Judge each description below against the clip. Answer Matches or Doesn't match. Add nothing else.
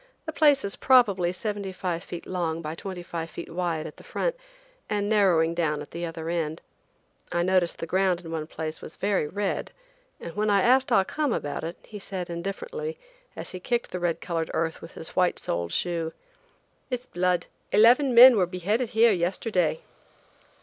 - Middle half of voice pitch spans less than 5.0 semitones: Matches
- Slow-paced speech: Doesn't match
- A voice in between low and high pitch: Matches